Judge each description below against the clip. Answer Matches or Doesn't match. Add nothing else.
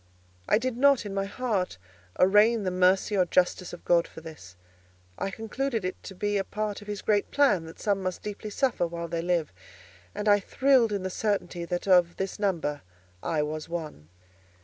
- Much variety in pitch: Doesn't match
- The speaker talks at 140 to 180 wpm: Doesn't match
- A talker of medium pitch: Doesn't match